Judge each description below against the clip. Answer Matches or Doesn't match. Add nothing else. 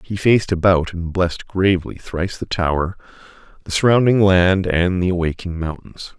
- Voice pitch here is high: Doesn't match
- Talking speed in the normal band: Matches